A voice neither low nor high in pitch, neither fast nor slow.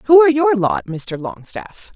No: very high, 250 Hz; average, 185 wpm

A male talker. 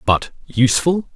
Yes: male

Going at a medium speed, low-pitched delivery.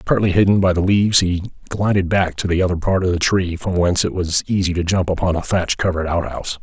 No: fast, 255 wpm; very low, 90 Hz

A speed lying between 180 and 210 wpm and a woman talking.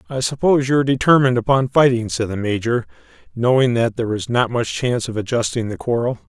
No: average, 200 wpm; male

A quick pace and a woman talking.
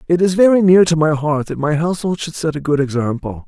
No: fast, 260 wpm; male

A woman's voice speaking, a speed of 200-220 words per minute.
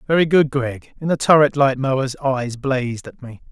No: male; fast, 205 wpm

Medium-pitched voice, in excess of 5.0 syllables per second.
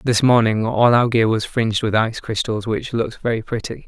No: low, 115 Hz; 5.6 syllables/s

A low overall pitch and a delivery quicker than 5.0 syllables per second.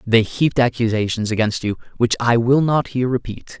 Yes: low, 120 Hz; 5.5 syllables/s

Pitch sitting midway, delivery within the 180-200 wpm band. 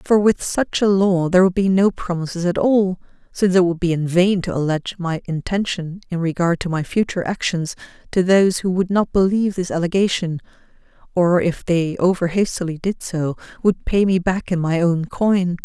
Yes: medium, 180 Hz; average, 195 wpm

